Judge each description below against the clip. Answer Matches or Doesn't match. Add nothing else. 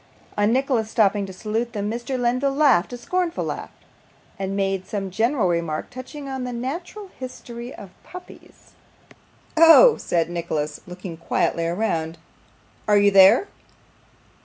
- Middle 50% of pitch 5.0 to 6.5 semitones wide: Matches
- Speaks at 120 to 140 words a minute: Matches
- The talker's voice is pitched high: Matches